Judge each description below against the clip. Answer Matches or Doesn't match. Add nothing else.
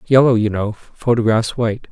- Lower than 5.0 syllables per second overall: Doesn't match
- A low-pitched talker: Matches